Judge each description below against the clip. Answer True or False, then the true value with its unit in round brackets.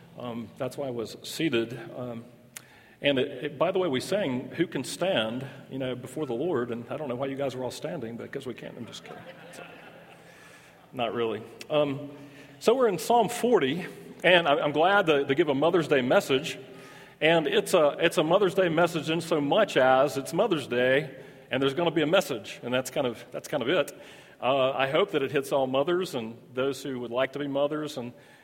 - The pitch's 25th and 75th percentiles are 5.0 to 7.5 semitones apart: False (3.8 semitones)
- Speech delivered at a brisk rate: True (225 wpm)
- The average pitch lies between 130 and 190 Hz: True (135 Hz)